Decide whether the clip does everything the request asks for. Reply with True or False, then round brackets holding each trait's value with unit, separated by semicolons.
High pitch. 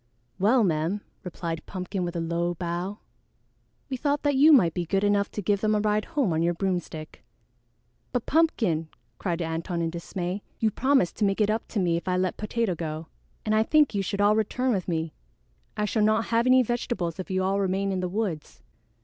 True (195 Hz)